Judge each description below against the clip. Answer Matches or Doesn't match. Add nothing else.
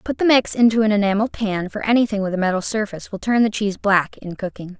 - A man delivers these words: Doesn't match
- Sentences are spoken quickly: Matches